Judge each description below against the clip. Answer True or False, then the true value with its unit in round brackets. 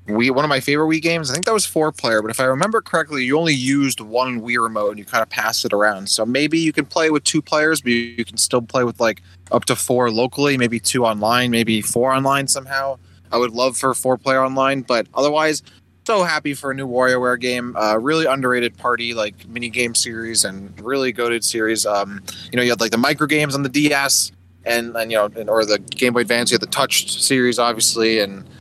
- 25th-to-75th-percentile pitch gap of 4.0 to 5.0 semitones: False (3.4 semitones)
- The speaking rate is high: True (240 wpm)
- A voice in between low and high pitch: False (125 Hz)